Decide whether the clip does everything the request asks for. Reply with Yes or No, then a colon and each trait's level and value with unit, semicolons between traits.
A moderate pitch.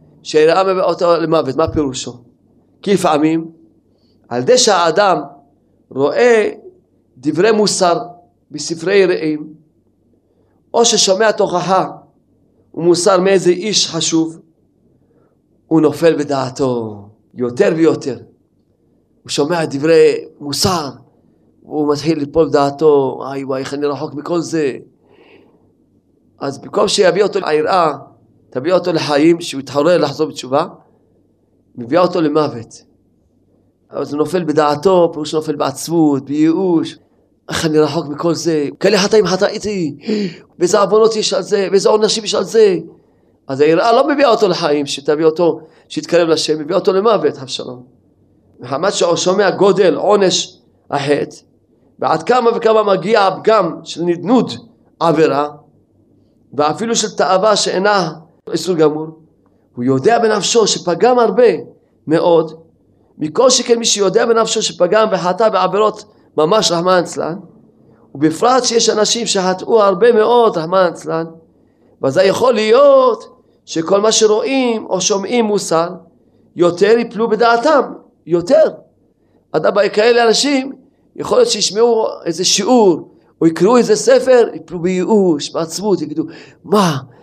Yes: medium, 175 Hz